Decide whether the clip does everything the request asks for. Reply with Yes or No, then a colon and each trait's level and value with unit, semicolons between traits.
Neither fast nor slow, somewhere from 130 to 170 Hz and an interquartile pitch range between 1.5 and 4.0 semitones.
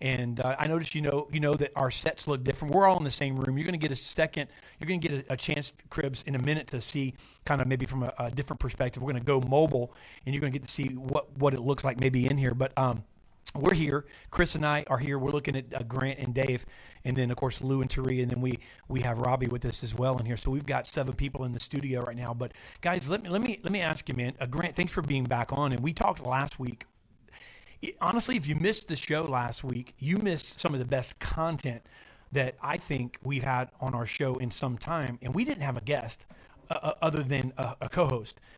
No: fast, 270 wpm; low, 135 Hz; average, 2.9 semitones